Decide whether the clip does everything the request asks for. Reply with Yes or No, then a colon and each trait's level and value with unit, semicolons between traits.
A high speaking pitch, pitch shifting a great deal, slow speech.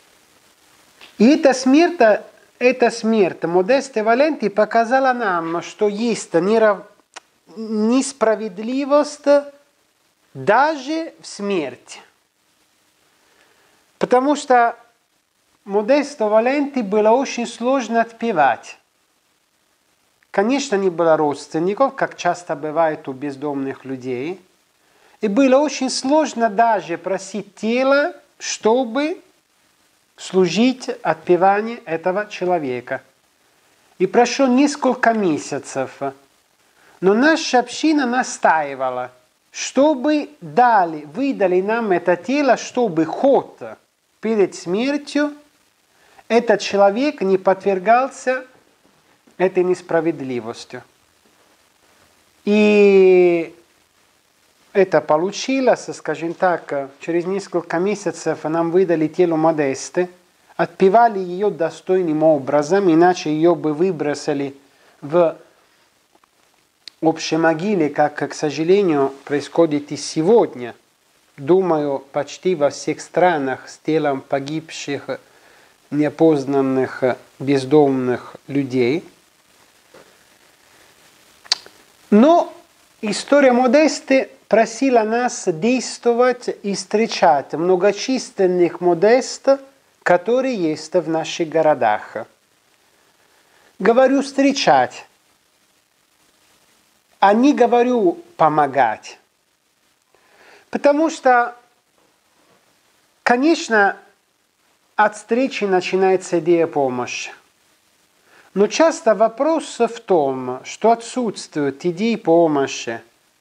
Yes: high, 200 Hz; wide, 7.3 semitones; slow, 80 wpm